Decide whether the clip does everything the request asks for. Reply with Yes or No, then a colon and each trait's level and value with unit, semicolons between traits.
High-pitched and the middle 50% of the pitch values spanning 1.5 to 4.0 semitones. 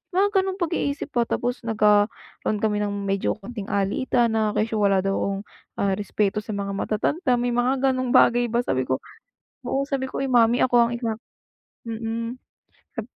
Yes: high, 230 Hz; average, 3.5 semitones